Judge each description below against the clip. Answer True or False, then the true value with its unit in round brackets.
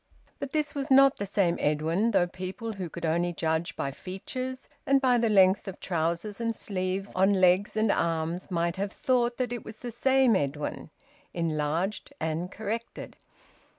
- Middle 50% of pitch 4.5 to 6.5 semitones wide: True (5.3 semitones)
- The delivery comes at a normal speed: True (170 wpm)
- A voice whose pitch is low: False (190 Hz)